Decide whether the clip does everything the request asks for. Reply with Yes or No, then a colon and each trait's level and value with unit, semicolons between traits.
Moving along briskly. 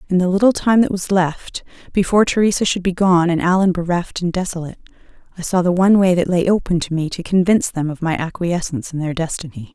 Yes: fast, 220 wpm